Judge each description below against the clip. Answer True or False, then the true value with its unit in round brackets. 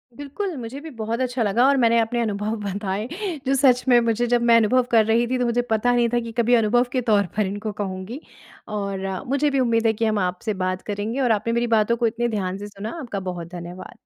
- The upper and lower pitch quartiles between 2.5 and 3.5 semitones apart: True (2.9 semitones)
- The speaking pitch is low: False (230 Hz)